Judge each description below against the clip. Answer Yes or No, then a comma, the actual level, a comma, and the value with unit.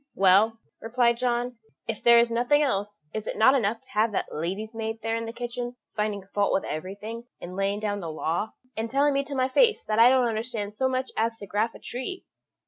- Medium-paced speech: No, fast, 225 wpm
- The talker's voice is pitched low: No, high, 225 Hz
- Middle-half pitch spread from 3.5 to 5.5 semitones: No, average, 3.0 semitones